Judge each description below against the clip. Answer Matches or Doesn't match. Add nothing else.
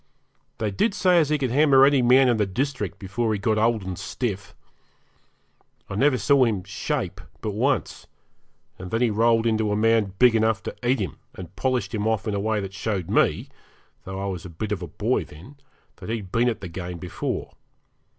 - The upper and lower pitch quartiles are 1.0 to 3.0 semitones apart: Doesn't match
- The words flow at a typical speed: Doesn't match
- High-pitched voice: Doesn't match